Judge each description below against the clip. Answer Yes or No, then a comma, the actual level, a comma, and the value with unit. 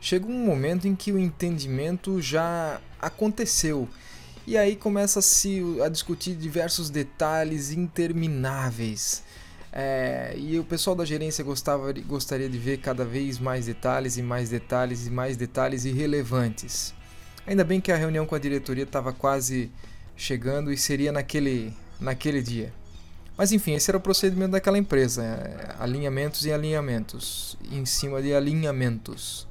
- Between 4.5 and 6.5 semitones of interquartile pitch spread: Yes, average, 5.2 semitones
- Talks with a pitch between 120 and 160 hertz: Yes, medium, 140 Hz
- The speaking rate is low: No, average, 140 wpm